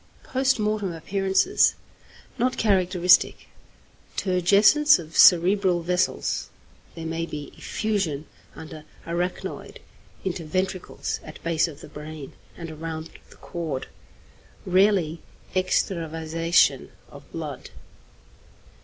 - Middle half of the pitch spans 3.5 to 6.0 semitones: No, average, 3.0 semitones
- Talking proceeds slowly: Yes, slow, 95 wpm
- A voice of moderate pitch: Yes, medium, 175 Hz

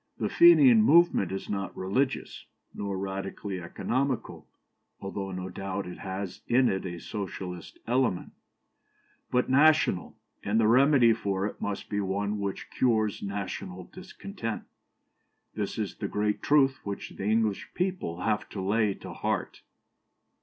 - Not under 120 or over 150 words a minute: Yes, average, 140 wpm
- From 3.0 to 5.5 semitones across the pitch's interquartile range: Yes, average, 4.7 semitones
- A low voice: Yes, low, 105 Hz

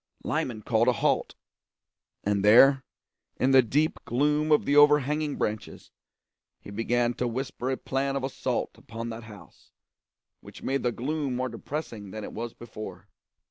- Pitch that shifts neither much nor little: Yes, average, 3.5 semitones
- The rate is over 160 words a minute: No, average, 155 wpm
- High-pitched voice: No, low, 125 Hz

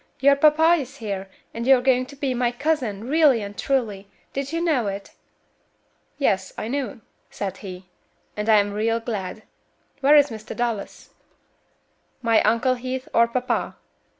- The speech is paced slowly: No, average, 155 wpm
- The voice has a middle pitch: No, high, 240 Hz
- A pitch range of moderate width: Yes, average, 4.5 semitones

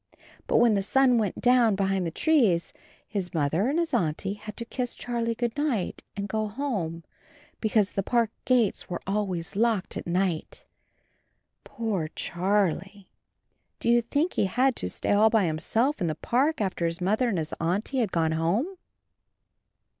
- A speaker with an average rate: Yes, average, 170 wpm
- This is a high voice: Yes, high, 210 Hz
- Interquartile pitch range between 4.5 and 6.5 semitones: Yes, average, 5.0 semitones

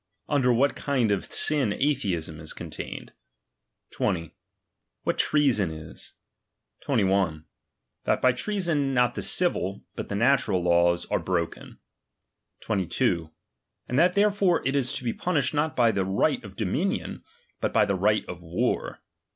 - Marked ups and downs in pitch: Yes, wide, 7.5 semitones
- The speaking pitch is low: Yes, low, 115 Hz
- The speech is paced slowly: No, average, 145 wpm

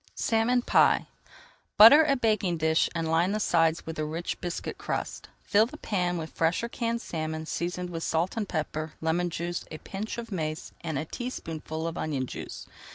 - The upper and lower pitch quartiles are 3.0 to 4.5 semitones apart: No, average, 5.1 semitones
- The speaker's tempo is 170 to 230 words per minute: Yes, average, 185 wpm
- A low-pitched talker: No, medium, 170 Hz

